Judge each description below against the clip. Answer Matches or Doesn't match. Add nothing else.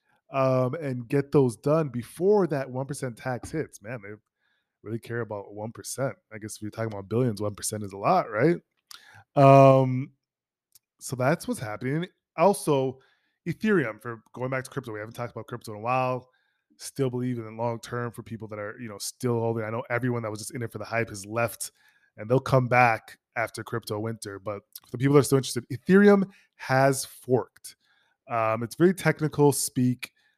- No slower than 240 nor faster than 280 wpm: Doesn't match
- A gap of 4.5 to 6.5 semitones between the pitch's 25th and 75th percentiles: Doesn't match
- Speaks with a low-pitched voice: Matches